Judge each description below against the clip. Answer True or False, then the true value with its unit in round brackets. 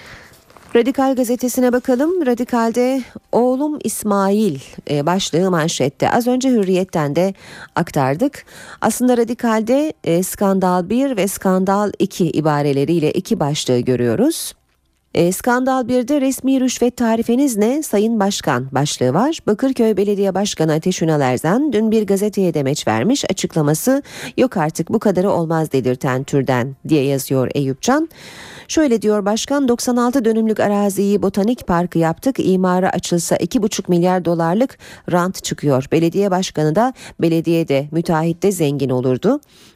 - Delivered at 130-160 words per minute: False (120 wpm)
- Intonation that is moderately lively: False (7.1 semitones)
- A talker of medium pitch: False (195 Hz)